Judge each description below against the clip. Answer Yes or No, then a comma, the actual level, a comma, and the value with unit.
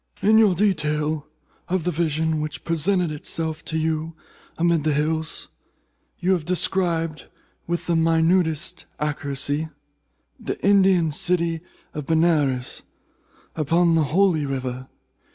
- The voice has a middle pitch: Yes, medium, 160 Hz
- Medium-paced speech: No, slow, 115 wpm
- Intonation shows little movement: Yes, narrow, 2.2 semitones